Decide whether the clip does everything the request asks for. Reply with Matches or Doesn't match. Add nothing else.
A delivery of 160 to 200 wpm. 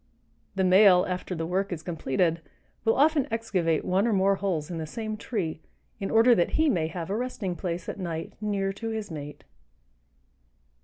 Matches